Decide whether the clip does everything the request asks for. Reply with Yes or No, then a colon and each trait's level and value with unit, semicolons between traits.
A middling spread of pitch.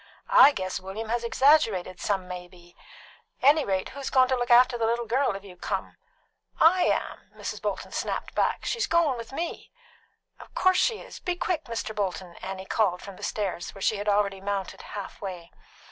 No: wide, 5.8 semitones